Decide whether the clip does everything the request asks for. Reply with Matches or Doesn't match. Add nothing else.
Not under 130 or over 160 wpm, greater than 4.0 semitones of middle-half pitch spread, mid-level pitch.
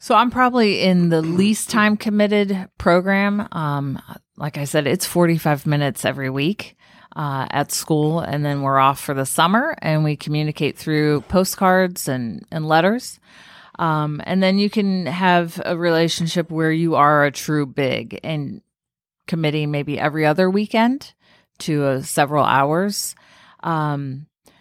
Matches